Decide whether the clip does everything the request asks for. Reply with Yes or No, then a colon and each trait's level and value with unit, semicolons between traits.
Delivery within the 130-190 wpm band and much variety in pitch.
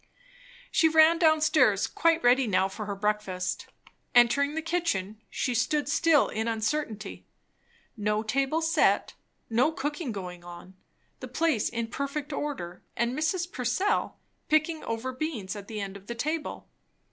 Yes: average, 145 wpm; wide, 6.6 semitones